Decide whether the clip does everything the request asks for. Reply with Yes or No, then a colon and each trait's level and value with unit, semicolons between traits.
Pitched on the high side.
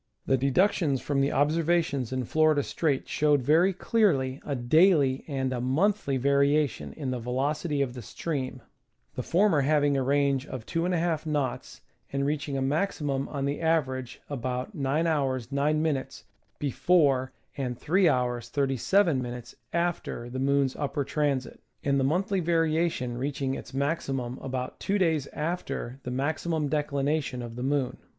No: medium, 140 Hz